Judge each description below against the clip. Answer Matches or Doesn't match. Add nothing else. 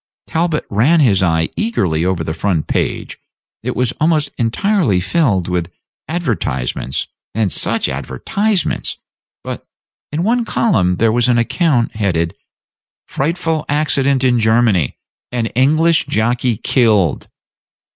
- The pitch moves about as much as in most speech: Doesn't match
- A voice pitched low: Matches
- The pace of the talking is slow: Matches